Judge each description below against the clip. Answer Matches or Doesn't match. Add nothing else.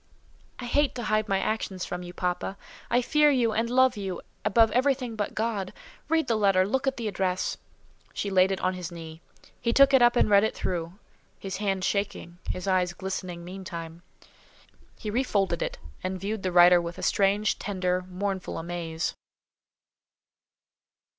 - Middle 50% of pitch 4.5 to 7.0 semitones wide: Doesn't match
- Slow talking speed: Doesn't match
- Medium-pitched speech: Doesn't match